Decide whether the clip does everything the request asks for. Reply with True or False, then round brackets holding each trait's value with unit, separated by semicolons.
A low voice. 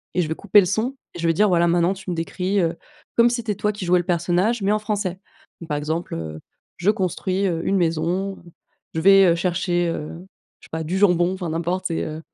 False (180 Hz)